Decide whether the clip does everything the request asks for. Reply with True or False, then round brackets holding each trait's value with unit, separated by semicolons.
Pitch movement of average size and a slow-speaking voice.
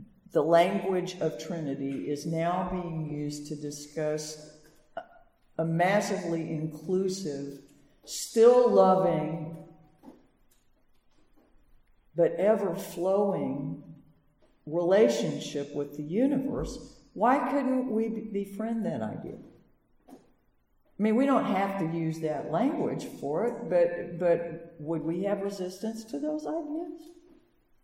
False (6.2 semitones; 105 wpm)